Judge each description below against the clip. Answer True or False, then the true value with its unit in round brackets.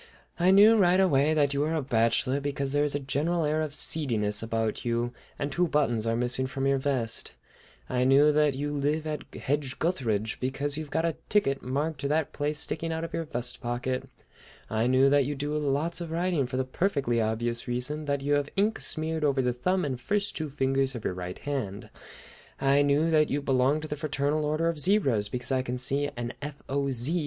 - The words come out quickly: True (215 wpm)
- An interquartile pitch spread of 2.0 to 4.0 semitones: True (3.3 semitones)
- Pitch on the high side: False (140 Hz)